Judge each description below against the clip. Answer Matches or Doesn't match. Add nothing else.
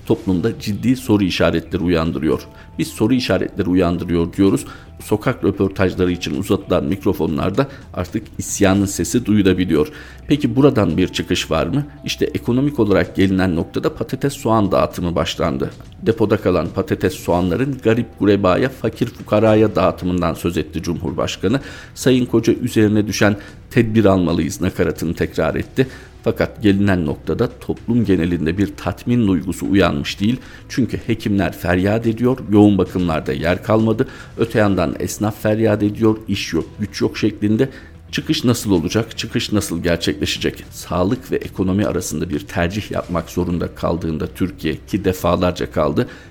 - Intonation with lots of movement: Doesn't match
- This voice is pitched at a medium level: Doesn't match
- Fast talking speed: Doesn't match